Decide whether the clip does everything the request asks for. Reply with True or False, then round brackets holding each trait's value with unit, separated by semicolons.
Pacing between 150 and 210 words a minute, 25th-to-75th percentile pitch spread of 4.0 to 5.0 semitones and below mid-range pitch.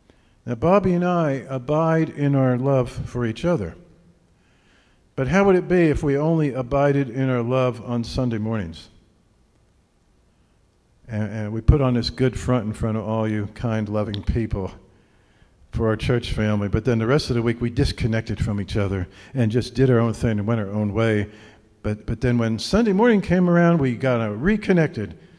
True (190 wpm; 4.4 semitones; 120 Hz)